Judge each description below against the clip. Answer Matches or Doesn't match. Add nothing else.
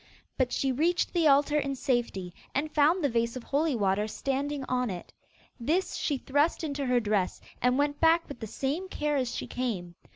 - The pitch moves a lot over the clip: Doesn't match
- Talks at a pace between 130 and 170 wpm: Doesn't match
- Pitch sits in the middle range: Doesn't match